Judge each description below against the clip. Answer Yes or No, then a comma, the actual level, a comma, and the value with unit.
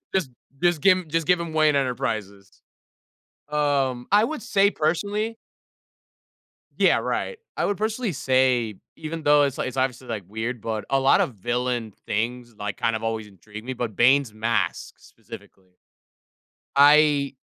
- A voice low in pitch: Yes, low, 130 Hz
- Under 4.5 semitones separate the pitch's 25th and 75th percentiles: No, wide, 5.6 semitones